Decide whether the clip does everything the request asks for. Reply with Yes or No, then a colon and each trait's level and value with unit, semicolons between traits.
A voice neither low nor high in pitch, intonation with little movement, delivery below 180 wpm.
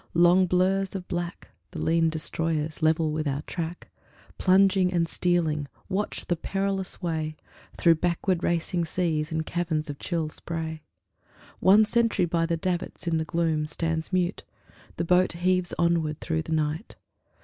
Yes: medium, 170 Hz; narrow, 2.2 semitones; average, 150 wpm